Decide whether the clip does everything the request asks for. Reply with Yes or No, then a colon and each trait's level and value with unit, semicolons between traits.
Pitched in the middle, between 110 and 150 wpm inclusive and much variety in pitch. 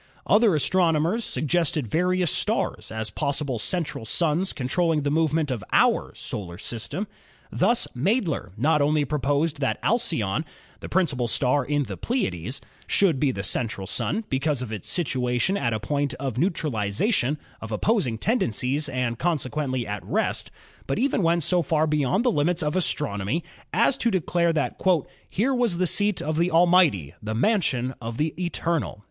No: medium, 150 Hz; average, 160 wpm; wide, 6.0 semitones